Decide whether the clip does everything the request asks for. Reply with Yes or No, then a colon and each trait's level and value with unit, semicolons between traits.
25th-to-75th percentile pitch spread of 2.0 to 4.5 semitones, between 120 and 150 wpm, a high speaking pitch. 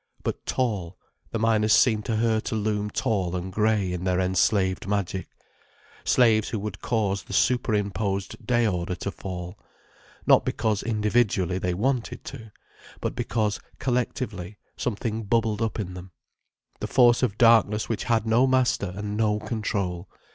No: average, 3.0 semitones; average, 145 wpm; low, 105 Hz